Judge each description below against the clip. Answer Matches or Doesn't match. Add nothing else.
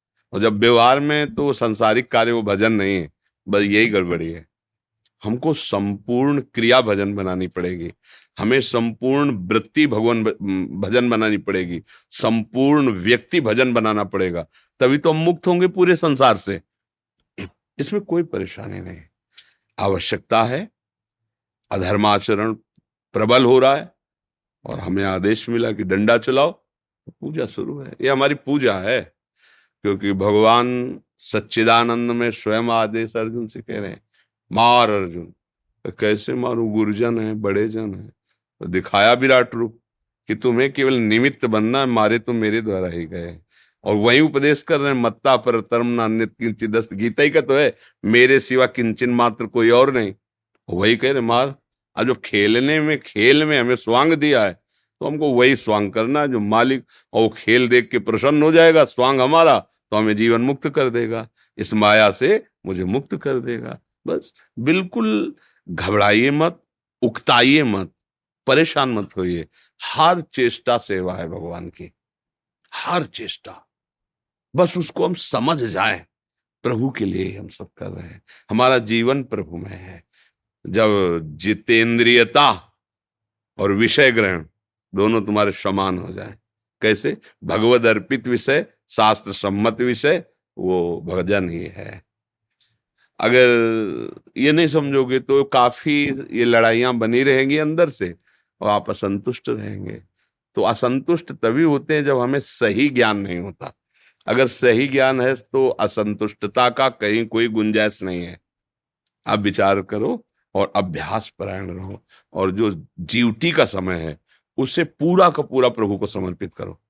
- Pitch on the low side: Matches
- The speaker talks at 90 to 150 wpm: Matches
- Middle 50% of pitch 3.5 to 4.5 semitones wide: Matches